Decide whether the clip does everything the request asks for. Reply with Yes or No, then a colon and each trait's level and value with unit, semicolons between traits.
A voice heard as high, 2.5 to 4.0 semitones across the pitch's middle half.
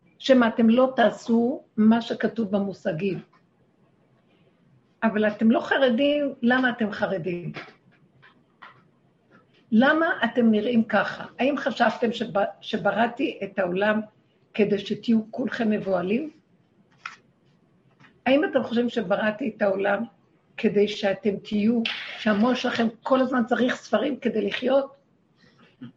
Yes: high, 225 Hz; average, 3.3 semitones